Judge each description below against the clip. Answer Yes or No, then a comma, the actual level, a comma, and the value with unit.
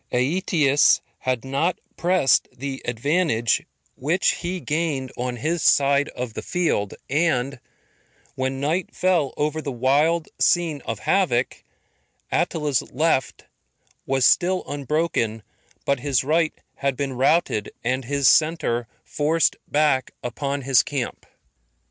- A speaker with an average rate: No, slow, 120 wpm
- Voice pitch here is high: No, medium, 140 Hz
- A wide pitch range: No, average, 3.9 semitones